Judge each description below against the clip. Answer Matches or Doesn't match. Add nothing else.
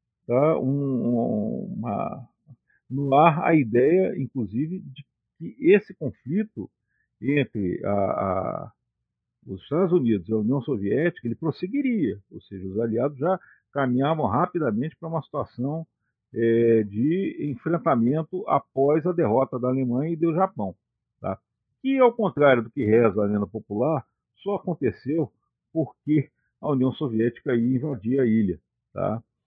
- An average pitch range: Doesn't match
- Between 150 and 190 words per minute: Doesn't match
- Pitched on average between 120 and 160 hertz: Matches